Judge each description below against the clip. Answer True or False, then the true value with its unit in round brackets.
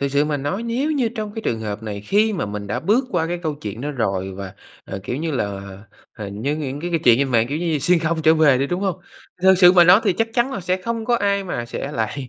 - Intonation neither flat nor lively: False (8.2 semitones)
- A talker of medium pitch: True (155 Hz)